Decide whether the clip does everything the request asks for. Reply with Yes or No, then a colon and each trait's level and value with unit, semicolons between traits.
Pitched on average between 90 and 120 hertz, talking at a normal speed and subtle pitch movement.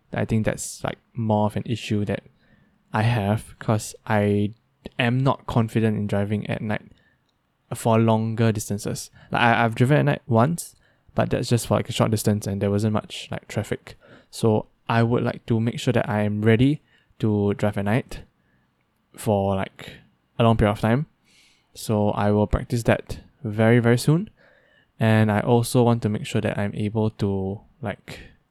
Yes: low, 110 Hz; average, 180 wpm; narrow, 2.3 semitones